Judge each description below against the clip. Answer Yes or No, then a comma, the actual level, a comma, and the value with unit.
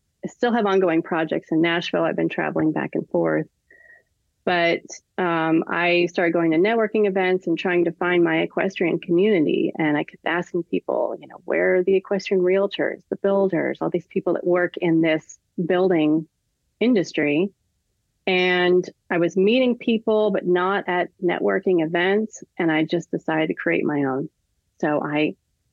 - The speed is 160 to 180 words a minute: Yes, average, 165 wpm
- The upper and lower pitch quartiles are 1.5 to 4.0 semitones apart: Yes, average, 2.9 semitones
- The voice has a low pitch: No, medium, 175 Hz